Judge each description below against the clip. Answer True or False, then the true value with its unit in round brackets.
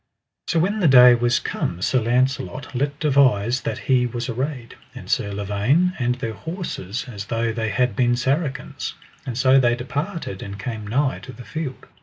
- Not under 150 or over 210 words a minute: True (180 wpm)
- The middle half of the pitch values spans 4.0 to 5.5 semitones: False (3.3 semitones)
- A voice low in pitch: True (125 Hz)